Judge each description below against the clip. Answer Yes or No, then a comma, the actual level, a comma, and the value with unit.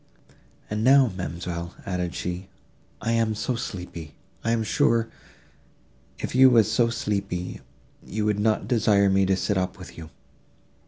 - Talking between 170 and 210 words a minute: No, average, 145 wpm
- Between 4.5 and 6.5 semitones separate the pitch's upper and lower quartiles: No, average, 4.0 semitones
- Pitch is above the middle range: No, low, 105 Hz